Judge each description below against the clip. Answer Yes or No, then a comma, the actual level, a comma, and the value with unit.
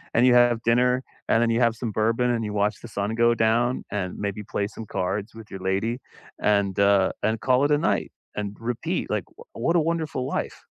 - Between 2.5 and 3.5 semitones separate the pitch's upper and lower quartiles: Yes, average, 2.9 semitones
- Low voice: Yes, low, 115 Hz